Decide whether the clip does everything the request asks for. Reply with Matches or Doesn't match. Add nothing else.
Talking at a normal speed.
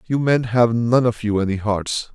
Doesn't match